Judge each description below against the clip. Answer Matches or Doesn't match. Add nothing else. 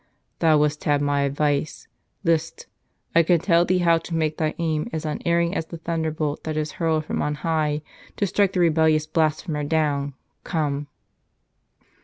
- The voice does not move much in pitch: Matches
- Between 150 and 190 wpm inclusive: Matches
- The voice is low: Doesn't match